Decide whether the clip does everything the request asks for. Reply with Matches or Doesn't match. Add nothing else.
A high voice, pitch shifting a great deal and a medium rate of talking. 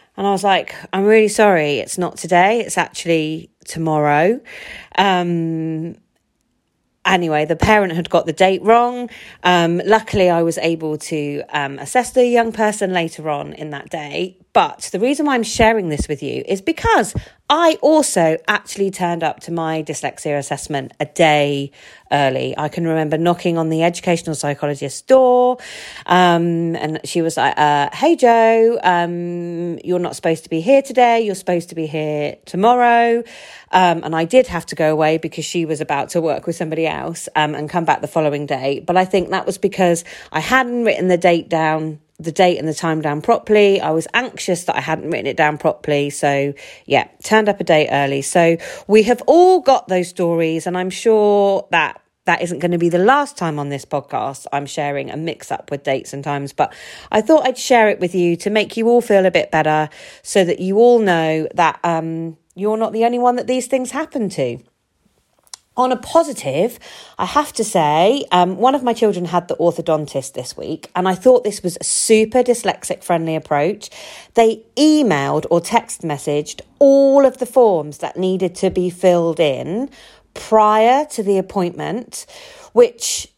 Doesn't match